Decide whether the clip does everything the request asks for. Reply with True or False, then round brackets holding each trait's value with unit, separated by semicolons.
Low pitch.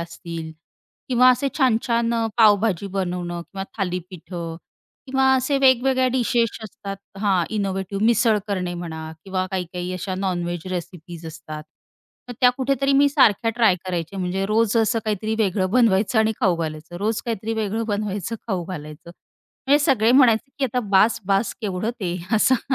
False (200 Hz)